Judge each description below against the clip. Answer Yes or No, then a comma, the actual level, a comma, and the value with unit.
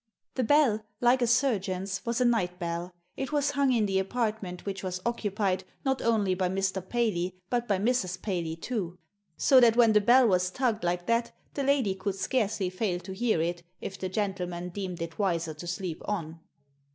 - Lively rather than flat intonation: No, average, 4.6 semitones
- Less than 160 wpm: No, average, 190 wpm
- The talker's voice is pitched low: No, high, 195 Hz